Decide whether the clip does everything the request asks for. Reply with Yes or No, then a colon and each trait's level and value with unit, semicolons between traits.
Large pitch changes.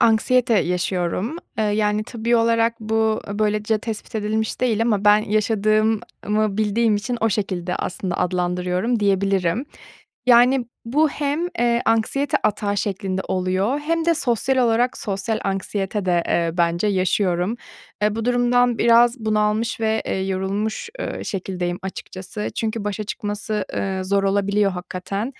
No: average, 3.0 semitones